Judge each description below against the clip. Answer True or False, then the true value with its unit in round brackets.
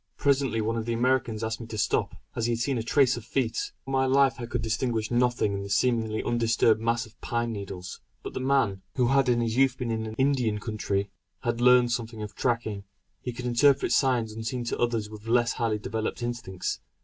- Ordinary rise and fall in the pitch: False (2.1 semitones)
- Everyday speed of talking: False (215 wpm)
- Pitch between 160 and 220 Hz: False (115 Hz)